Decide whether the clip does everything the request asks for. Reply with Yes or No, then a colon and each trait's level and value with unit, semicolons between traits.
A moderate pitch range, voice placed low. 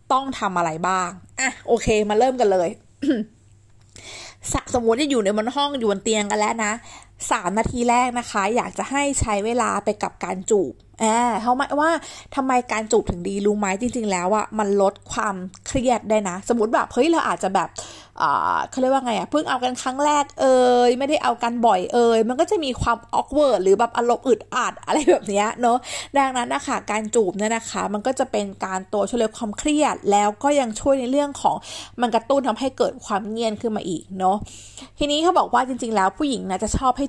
No: average, 4.1 semitones; high, 235 Hz